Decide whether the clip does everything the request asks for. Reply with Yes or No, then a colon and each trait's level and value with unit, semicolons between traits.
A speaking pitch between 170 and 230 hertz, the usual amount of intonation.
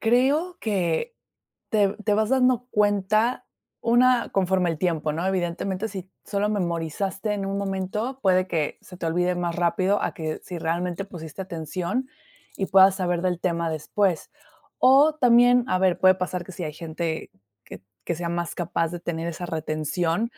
Yes: medium, 185 Hz; average, 3.6 semitones